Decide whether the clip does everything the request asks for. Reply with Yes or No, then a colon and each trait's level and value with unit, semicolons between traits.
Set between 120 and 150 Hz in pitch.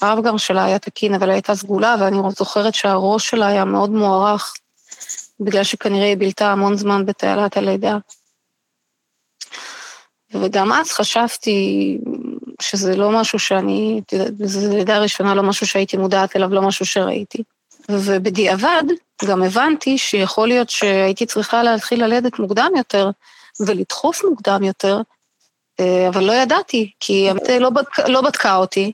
No: high, 205 Hz